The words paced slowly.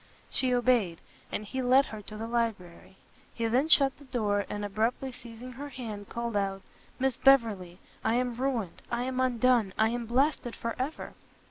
No: average, 175 wpm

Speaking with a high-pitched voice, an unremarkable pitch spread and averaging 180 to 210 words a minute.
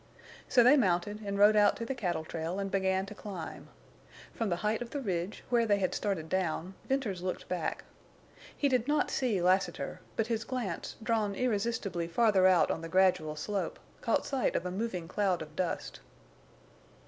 Yes: high, 195 Hz; average, 4.1 semitones; average, 185 wpm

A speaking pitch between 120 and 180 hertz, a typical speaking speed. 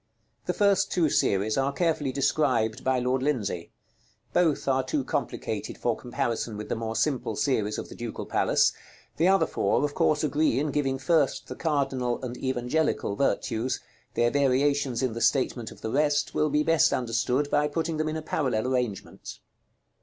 Yes: low, 135 Hz; average, 175 wpm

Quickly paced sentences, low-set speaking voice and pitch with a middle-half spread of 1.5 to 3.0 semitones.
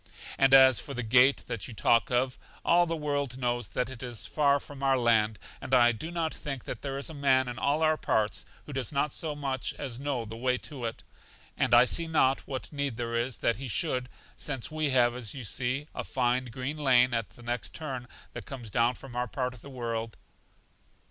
Yes: fast, 220 wpm; low, 130 Hz; average, 2.7 semitones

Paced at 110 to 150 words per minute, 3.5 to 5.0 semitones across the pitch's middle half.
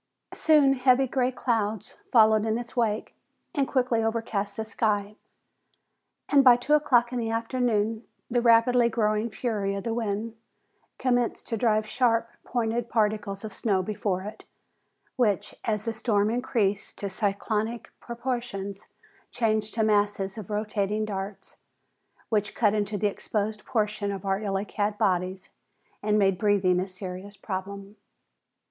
No: average, 140 wpm; narrow, 2.6 semitones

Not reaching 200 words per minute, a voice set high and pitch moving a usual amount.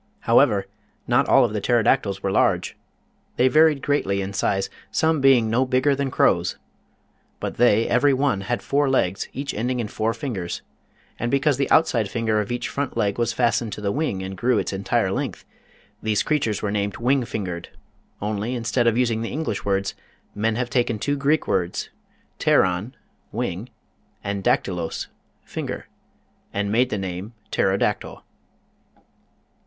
No: average, 165 wpm; low, 115 Hz; average, 4.6 semitones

